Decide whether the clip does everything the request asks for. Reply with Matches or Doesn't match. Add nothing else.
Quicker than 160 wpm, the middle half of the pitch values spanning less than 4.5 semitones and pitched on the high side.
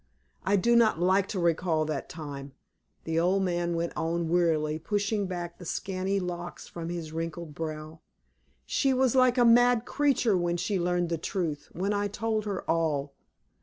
Doesn't match